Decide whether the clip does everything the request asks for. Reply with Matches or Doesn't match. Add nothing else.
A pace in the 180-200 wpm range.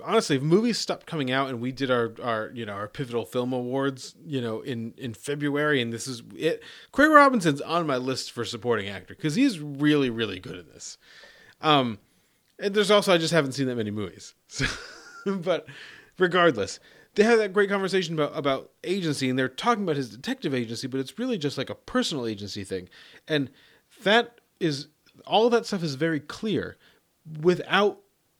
Matches